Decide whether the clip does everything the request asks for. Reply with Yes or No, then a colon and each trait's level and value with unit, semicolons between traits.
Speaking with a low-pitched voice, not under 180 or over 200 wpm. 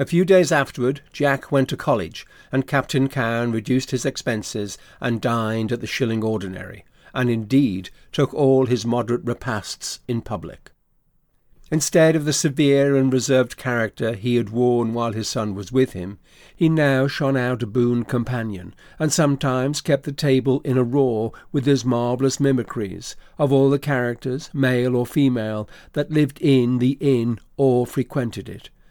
No: low, 130 Hz; average, 165 wpm